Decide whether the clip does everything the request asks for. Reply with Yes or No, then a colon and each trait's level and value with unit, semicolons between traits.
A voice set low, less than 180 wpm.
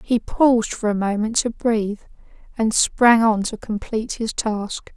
No: high, 220 Hz; average, 170 wpm